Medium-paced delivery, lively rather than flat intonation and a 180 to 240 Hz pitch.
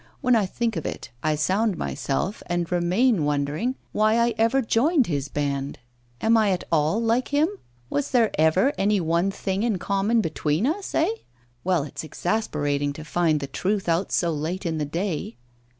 Yes: average, 180 wpm; wide, 6.6 semitones; medium, 185 Hz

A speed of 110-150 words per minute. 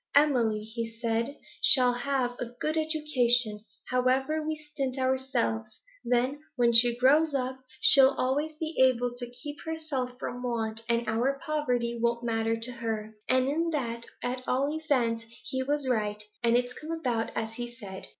No: average, 160 wpm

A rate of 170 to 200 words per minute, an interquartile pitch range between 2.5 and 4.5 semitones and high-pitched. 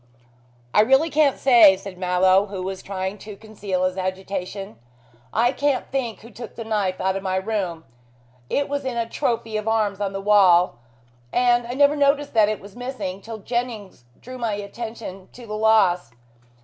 Yes: average, 180 wpm; average, 4.0 semitones; high, 210 Hz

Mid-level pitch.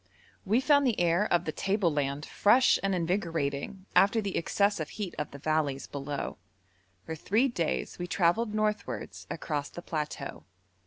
Yes: medium, 175 Hz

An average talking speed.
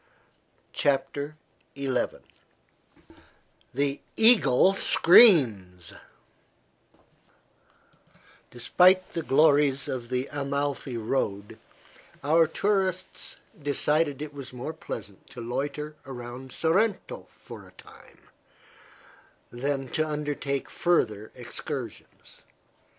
No: slow, 80 wpm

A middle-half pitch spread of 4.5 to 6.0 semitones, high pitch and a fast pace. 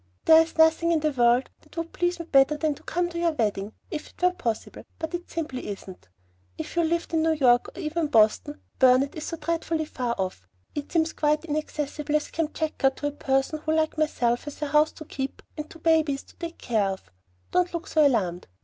No: average, 3.7 semitones; very high, 305 Hz; fast, 225 wpm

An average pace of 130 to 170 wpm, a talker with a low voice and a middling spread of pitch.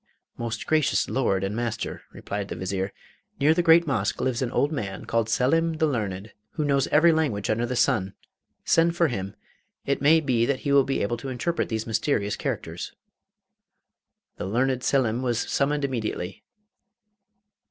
Yes: average, 165 wpm; low, 125 Hz; average, 5.0 semitones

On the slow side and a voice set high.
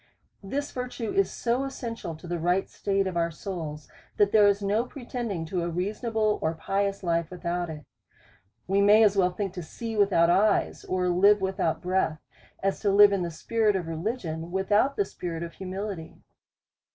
No: average, 180 wpm; high, 195 Hz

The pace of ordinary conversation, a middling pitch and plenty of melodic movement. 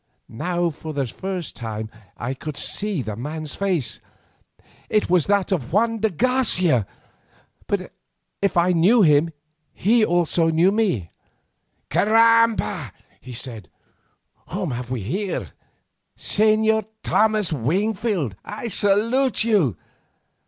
No: slow, 115 wpm; medium, 180 Hz; wide, 6.9 semitones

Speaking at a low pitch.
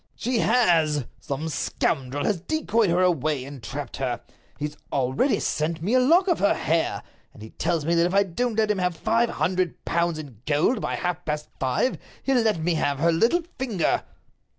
No: medium, 170 Hz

